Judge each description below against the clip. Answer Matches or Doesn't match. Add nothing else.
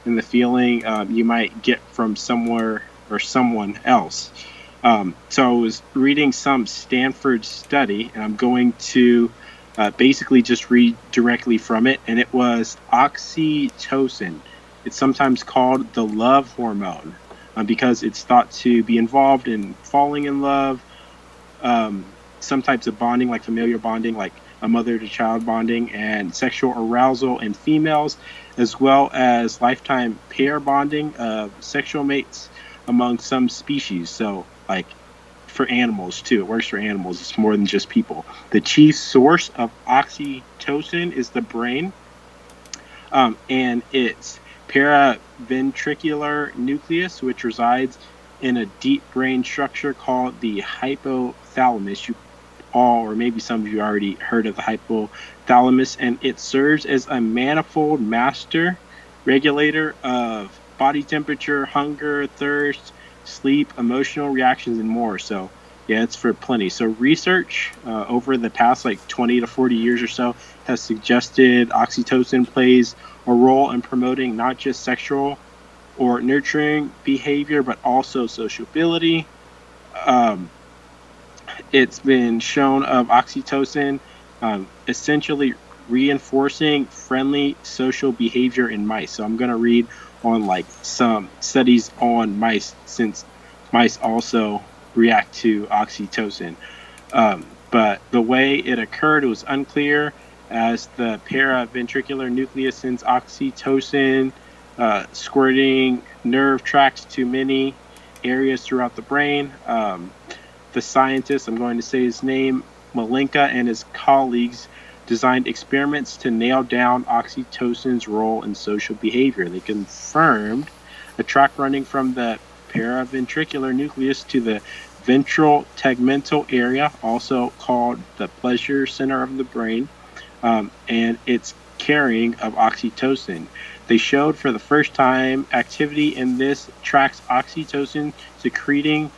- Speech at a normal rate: Doesn't match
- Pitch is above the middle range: Doesn't match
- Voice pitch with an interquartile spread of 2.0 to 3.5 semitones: Matches